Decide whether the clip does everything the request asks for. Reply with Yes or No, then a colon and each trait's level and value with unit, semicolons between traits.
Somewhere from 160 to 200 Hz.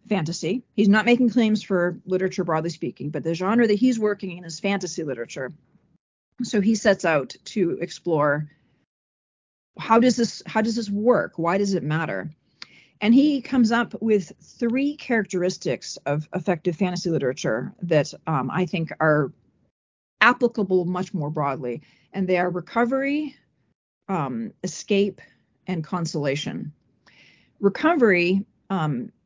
Yes: medium, 185 Hz